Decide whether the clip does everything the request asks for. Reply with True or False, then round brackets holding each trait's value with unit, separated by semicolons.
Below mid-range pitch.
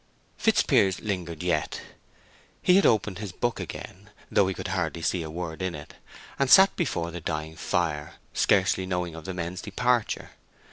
True (90 Hz)